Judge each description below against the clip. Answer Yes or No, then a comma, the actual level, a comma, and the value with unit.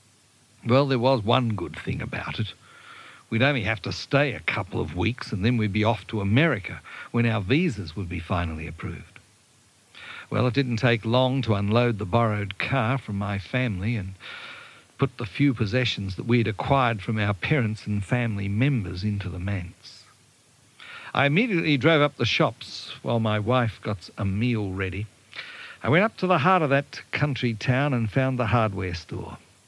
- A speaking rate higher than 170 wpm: Yes, average, 180 wpm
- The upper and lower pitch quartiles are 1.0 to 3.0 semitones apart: No, average, 4.0 semitones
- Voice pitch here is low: Yes, low, 115 Hz